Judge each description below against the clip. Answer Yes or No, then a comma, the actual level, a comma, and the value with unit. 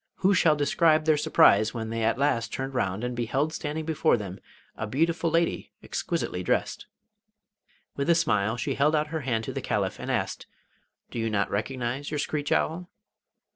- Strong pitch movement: Yes, wide, 5.7 semitones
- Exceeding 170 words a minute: Yes, average, 180 wpm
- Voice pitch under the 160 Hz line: Yes, medium, 140 Hz